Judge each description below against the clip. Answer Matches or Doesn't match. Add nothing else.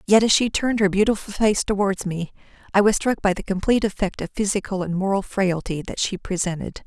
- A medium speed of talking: Doesn't match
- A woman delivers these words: Matches